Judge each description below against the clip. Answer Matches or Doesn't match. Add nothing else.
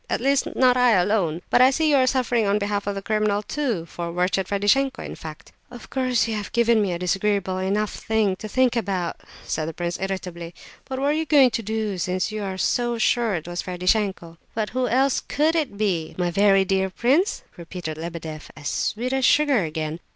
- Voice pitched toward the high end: Matches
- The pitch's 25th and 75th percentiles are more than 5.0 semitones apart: Matches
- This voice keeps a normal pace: Doesn't match